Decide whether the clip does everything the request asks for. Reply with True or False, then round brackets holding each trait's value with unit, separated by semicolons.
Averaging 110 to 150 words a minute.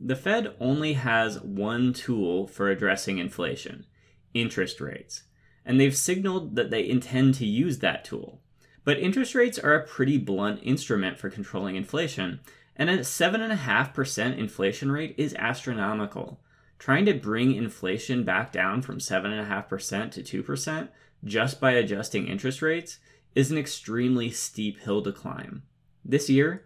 True (140 wpm)